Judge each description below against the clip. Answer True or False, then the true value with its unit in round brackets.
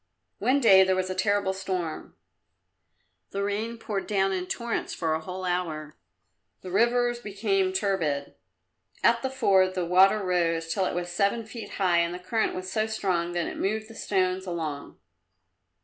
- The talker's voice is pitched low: False (190 Hz)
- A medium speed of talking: True (170 wpm)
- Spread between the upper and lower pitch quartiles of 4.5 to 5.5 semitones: False (3.1 semitones)